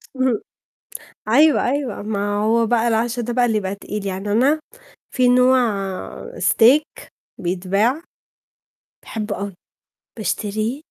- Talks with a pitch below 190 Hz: No, high, 225 Hz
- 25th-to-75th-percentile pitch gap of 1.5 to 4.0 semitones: Yes, average, 3.6 semitones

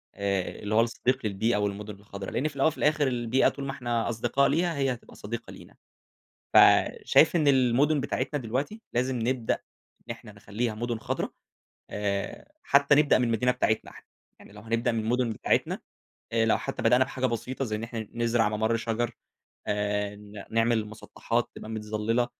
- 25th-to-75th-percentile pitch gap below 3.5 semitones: Yes, average, 3.1 semitones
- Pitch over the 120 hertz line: No, low, 115 Hz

